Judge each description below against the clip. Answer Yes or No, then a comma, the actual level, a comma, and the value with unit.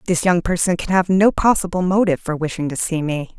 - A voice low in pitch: No, medium, 175 Hz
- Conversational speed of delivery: No, fast, 230 wpm